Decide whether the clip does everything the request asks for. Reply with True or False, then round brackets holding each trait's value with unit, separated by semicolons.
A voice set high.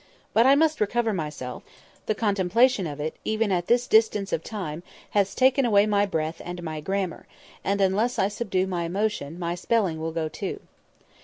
True (195 Hz)